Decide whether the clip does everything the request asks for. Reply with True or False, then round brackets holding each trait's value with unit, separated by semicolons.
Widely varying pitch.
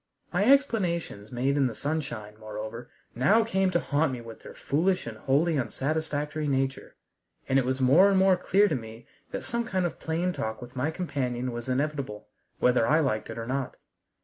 True (5.8 semitones)